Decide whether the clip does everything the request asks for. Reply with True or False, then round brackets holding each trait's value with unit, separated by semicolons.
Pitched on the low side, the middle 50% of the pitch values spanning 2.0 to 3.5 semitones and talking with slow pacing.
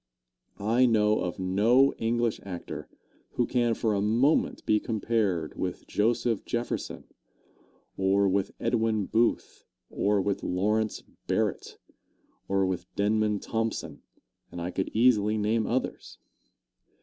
True (105 Hz; 2.9 semitones; 120 wpm)